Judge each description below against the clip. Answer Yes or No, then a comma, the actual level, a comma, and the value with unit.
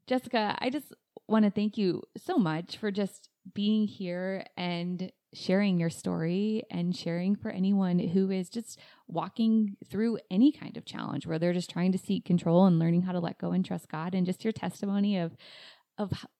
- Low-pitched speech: No, high, 190 Hz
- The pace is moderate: Yes, average, 190 wpm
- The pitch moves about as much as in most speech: Yes, average, 3.0 semitones